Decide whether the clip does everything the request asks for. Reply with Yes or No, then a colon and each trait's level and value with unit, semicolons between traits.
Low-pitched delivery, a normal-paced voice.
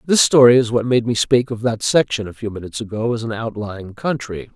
No: low, 115 Hz; fast, 235 wpm